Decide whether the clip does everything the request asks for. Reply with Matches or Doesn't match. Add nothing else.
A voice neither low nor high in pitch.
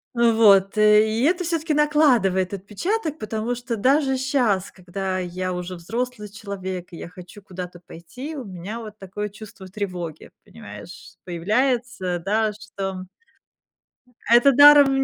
Doesn't match